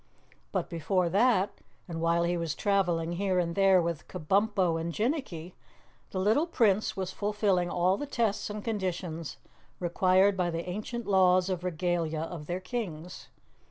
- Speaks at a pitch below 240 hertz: Yes, medium, 185 Hz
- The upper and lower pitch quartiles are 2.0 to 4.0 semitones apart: Yes, average, 3.0 semitones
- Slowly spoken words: No, average, 155 wpm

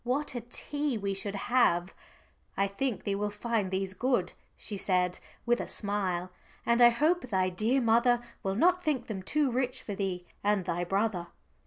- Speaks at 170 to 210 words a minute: Yes, average, 180 wpm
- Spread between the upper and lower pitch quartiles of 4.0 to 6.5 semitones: Yes, average, 4.4 semitones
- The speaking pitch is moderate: No, high, 210 Hz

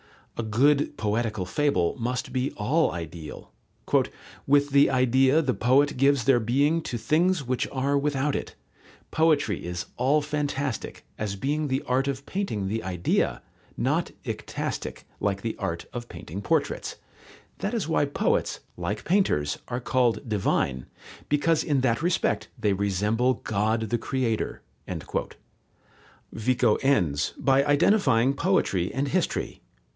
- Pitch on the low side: Yes, low, 130 Hz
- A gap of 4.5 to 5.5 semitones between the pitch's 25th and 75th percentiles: Yes, average, 4.9 semitones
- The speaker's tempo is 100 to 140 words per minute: Yes, slow, 135 wpm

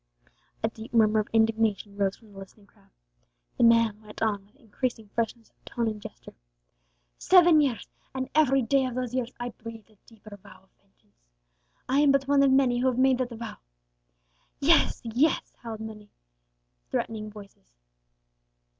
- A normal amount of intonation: Yes, average, 3.3 semitones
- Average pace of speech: Yes, average, 175 wpm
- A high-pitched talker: Yes, high, 225 Hz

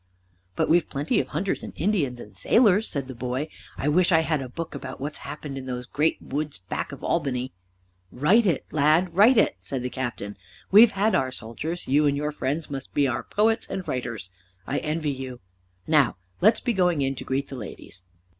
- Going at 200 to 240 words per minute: Yes, fast, 205 wpm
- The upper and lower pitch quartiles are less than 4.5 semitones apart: No, average, 4.8 semitones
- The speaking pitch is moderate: Yes, medium, 145 Hz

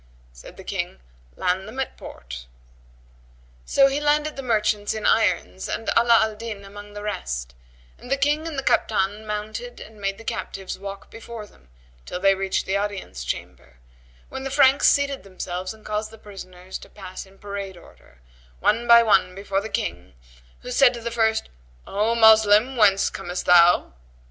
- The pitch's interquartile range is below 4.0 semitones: Yes, average, 3.4 semitones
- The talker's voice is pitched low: No, high, 210 Hz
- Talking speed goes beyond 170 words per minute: Yes, average, 180 wpm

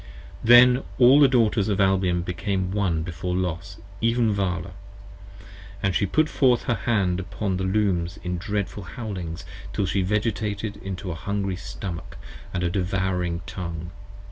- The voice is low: Yes, very low, 95 Hz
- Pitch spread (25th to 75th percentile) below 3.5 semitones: Yes, average, 2.8 semitones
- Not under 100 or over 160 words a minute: Yes, average, 145 wpm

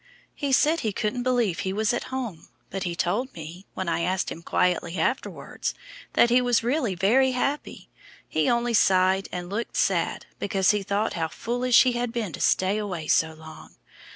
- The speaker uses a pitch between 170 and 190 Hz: No, high, 205 Hz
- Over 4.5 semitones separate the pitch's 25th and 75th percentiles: Yes, average, 5.3 semitones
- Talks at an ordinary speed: Yes, average, 185 wpm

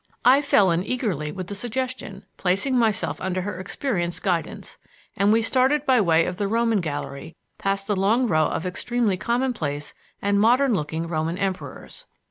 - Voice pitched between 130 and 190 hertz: No, high, 200 Hz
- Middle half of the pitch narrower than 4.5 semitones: No, wide, 5.5 semitones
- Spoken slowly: No, average, 165 wpm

